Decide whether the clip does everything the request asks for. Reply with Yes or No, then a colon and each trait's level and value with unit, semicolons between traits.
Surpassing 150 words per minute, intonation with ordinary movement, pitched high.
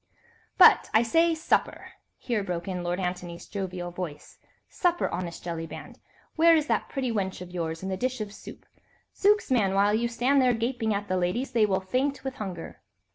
No: average, 185 wpm; wide, 6.1 semitones; high, 205 Hz